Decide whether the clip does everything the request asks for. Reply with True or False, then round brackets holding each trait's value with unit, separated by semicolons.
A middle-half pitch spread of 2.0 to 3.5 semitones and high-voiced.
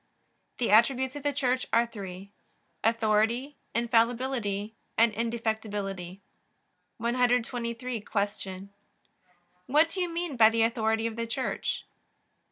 True (2.7 semitones; 230 Hz)